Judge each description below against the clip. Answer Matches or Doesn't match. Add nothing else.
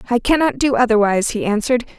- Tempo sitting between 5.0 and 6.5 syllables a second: Doesn't match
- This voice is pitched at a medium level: Doesn't match